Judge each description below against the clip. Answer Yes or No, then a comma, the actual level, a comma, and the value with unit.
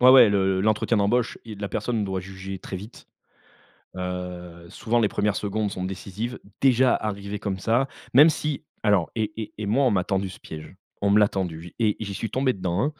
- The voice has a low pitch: Yes, low, 100 Hz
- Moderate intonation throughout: Yes, average, 3.2 semitones